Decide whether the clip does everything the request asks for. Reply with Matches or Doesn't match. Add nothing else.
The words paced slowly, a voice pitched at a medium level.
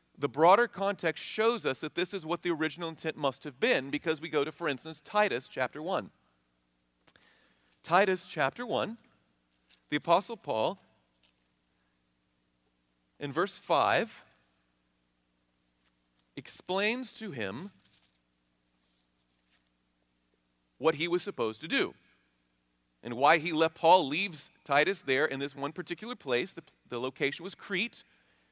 Doesn't match